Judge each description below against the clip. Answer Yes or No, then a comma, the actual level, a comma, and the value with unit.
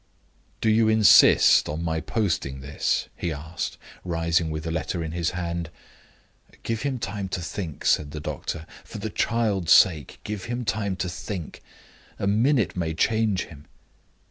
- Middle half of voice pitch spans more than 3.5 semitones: Yes, average, 4.7 semitones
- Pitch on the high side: No, very low, 90 Hz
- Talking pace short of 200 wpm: Yes, average, 160 wpm